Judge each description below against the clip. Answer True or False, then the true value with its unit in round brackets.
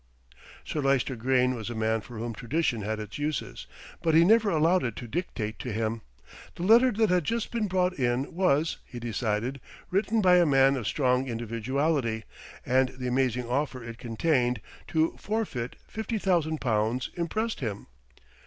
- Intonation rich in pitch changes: True (6.4 semitones)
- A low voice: True (130 Hz)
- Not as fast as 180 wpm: True (170 wpm)